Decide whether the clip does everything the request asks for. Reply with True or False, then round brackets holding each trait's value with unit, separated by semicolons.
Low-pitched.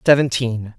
True (125 Hz)